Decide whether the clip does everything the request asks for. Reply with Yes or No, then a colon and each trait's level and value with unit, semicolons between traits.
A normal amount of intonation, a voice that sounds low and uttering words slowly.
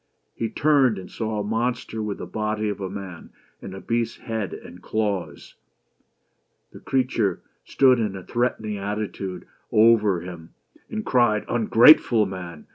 No: average, 3.2 semitones; low, 105 Hz; average, 145 wpm